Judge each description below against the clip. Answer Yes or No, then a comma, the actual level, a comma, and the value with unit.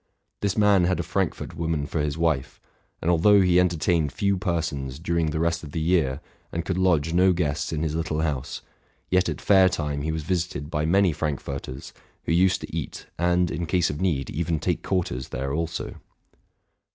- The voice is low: Yes, very low, 85 Hz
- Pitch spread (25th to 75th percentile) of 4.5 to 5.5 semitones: No, average, 3.2 semitones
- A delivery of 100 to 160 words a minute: No, average, 190 wpm